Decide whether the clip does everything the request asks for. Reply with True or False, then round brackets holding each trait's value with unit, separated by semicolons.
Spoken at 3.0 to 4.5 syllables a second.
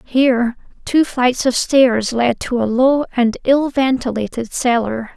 True (3.9 syllables/s)